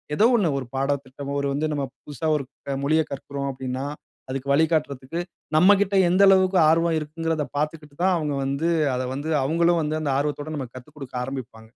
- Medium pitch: Yes, medium, 150 Hz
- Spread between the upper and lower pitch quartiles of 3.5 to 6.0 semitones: No, average, 3.0 semitones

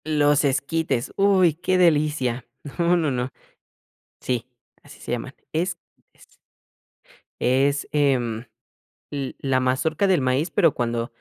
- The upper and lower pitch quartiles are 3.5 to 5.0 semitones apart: Yes, average, 4.2 semitones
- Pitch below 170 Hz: Yes, medium, 140 Hz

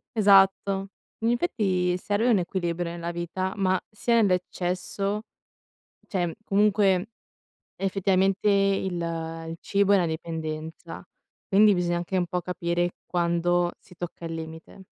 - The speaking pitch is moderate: Yes, medium, 180 Hz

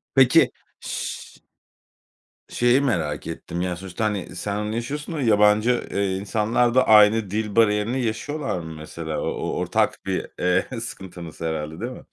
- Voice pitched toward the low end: Yes, low, 105 Hz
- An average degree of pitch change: Yes, average, 4.9 semitones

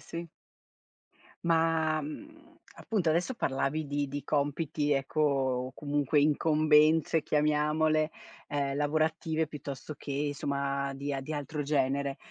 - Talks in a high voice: No, medium, 150 Hz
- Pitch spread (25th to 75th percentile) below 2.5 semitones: Yes, narrow, 2.0 semitones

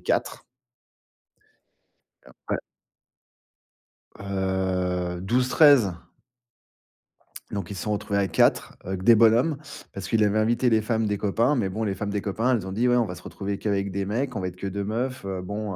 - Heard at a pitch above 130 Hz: No, low, 105 Hz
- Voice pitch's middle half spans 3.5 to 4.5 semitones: No, average, 3.0 semitones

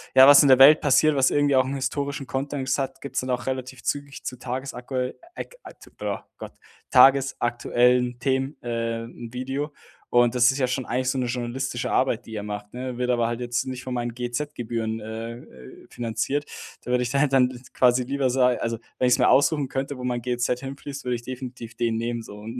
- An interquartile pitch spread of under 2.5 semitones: Yes, narrow, 1.9 semitones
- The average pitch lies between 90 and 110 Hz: No, low, 125 Hz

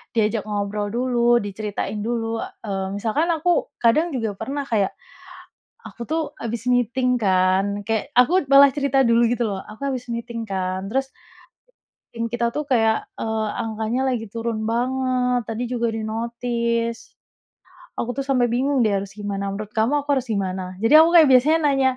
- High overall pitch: Yes, high, 235 Hz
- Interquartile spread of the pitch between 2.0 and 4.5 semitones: Yes, average, 3.1 semitones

